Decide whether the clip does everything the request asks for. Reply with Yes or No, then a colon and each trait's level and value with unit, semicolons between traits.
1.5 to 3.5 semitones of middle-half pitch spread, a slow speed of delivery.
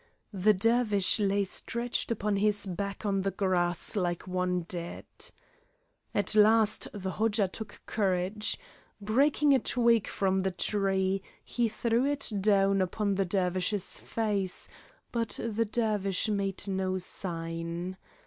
Yes: narrow, 2.6 semitones; slow, 130 wpm